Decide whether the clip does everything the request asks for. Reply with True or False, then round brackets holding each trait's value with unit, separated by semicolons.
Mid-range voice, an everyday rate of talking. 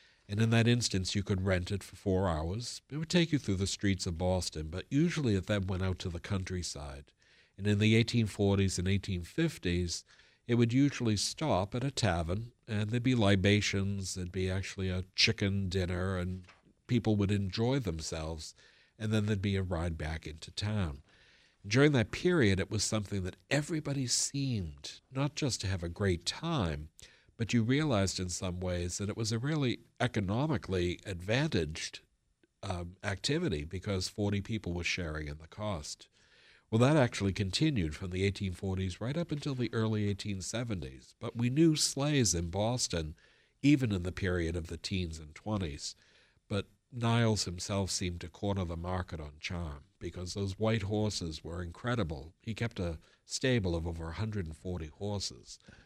False (100 Hz; 170 wpm)